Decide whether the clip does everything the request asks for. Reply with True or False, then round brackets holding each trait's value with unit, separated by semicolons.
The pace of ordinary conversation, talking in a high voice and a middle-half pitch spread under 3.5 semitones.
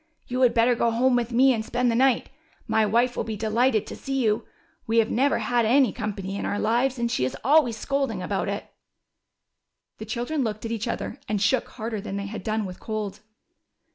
False (215 wpm; 230 Hz; 2.5 semitones)